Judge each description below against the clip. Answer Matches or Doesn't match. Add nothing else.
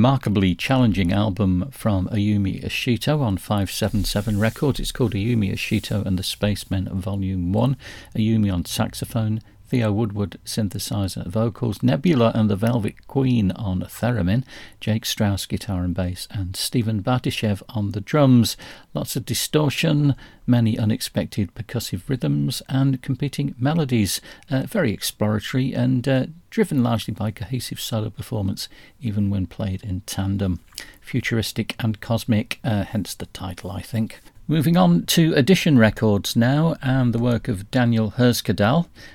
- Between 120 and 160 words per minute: Matches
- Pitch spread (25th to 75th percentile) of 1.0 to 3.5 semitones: Doesn't match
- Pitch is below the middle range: Matches